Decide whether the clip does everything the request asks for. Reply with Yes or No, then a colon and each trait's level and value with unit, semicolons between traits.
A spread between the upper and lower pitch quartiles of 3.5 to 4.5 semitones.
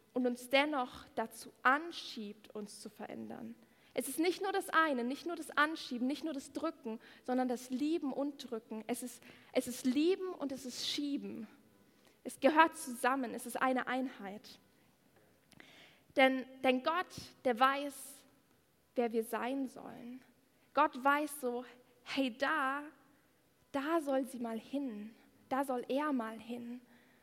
No: average, 2.7 semitones